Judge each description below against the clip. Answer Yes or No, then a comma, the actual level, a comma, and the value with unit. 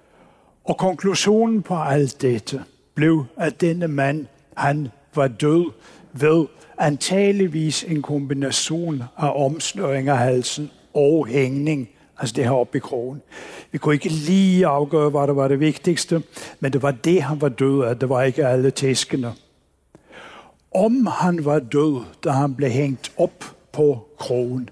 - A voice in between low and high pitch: Yes, medium, 145 Hz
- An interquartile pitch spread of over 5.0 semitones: No, average, 2.9 semitones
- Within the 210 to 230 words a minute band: No, average, 150 wpm